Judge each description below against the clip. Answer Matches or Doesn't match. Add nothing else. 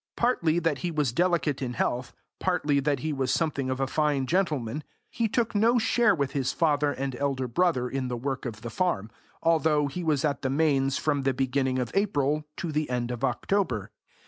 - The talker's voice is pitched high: Doesn't match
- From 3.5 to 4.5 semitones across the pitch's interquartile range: Matches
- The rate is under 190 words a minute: Doesn't match